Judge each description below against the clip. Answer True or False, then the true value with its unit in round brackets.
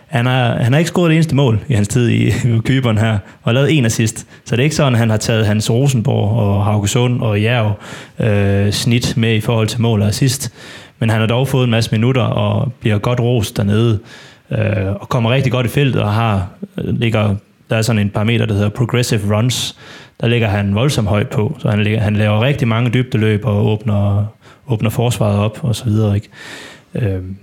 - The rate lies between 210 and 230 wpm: True (215 wpm)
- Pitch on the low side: True (115 Hz)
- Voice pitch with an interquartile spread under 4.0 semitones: True (3.1 semitones)